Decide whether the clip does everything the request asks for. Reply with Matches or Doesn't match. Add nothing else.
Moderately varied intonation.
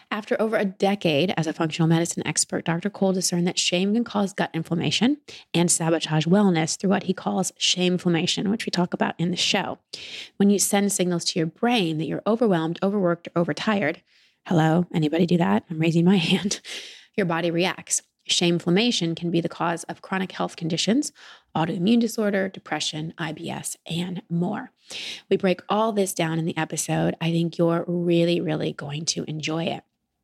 Matches